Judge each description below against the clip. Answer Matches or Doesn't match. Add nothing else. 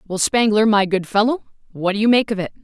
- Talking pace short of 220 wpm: Doesn't match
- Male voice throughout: Doesn't match